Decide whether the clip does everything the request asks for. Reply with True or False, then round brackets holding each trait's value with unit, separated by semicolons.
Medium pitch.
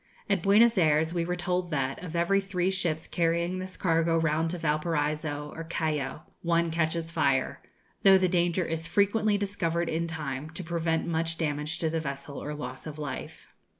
True (165 Hz)